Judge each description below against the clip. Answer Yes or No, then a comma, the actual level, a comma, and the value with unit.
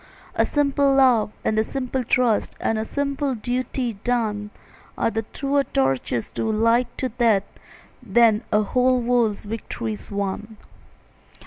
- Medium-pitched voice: No, high, 230 Hz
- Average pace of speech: No, slow, 130 wpm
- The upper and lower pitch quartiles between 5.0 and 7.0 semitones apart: No, average, 3.0 semitones